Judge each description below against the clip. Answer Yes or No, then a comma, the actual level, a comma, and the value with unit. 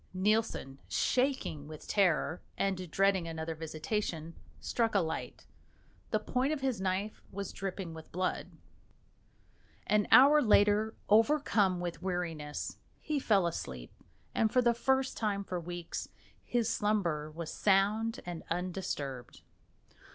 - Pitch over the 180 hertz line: Yes, high, 190 Hz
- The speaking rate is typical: No, slow, 125 wpm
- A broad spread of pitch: No, average, 4.8 semitones